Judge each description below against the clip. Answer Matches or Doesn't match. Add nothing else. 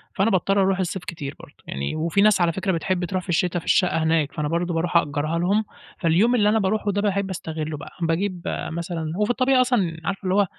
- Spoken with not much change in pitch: Doesn't match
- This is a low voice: Doesn't match